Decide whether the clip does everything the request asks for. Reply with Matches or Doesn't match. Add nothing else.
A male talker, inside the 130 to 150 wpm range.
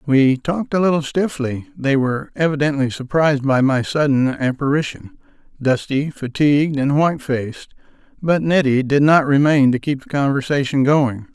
Matches